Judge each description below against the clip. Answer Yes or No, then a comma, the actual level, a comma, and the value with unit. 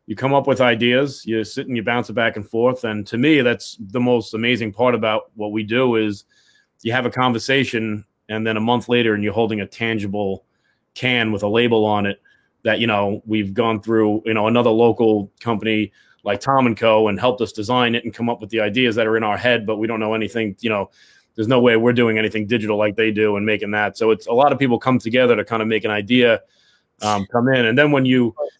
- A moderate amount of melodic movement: No, narrow, 2.2 semitones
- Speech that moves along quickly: Yes, fast, 250 wpm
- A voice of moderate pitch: No, low, 115 Hz